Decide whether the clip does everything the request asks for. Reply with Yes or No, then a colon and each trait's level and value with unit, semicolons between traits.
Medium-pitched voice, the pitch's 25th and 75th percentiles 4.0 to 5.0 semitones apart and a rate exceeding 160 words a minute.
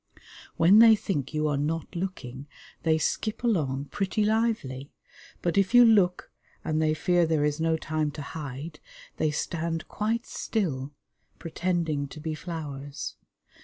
No: medium, 160 Hz; average, 4.3 semitones; average, 145 wpm